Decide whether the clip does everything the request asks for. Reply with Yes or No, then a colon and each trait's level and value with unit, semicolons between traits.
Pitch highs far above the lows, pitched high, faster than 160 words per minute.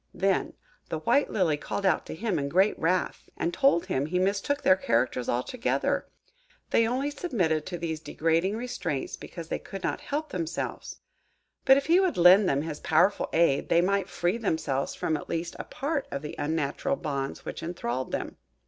No: wide, 6.0 semitones; medium, 175 Hz; average, 185 wpm